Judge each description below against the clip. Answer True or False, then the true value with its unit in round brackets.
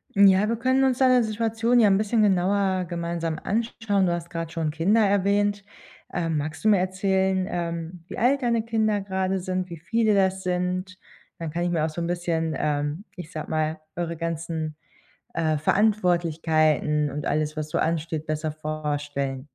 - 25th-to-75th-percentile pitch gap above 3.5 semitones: True (4.2 semitones)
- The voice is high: False (175 Hz)